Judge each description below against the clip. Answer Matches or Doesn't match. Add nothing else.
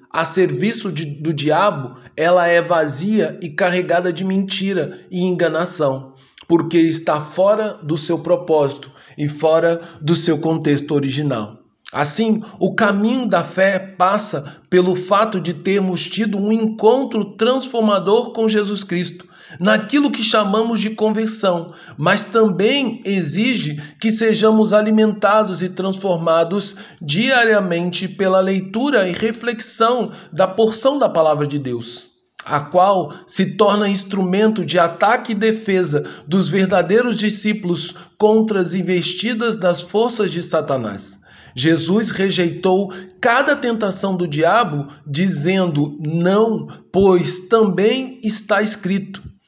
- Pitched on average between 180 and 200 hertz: Matches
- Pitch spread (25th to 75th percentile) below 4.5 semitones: Matches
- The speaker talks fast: Doesn't match